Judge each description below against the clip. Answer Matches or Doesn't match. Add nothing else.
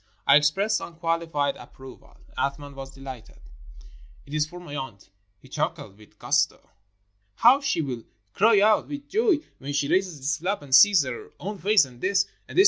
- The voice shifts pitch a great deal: Matches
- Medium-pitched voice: Matches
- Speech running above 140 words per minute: Matches